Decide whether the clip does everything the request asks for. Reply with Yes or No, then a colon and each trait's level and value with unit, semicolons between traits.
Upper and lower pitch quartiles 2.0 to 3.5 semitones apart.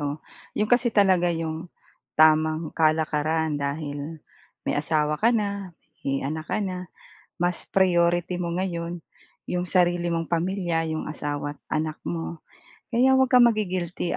Yes: average, 2.9 semitones